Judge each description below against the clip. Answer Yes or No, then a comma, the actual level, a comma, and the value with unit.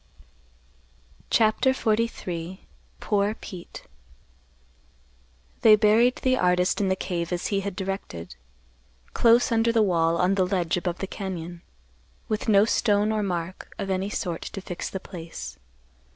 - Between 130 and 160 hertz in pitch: No, high, 195 Hz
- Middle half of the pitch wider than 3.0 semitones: Yes, average, 3.4 semitones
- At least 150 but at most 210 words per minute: No, slow, 135 wpm